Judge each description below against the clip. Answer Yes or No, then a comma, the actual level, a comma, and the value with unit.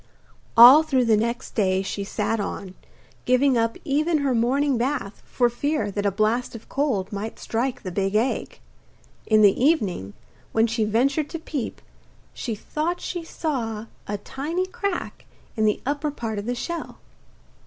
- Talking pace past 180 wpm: No, average, 165 wpm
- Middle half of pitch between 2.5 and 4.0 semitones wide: No, average, 5.0 semitones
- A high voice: Yes, high, 235 Hz